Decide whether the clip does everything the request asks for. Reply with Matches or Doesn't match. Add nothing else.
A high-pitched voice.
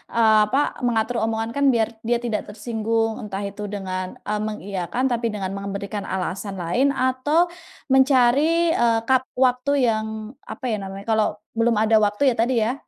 Matches